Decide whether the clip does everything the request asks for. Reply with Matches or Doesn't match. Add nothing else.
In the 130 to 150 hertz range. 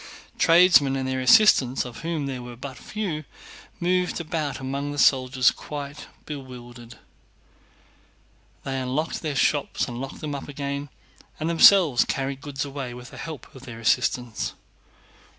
Matches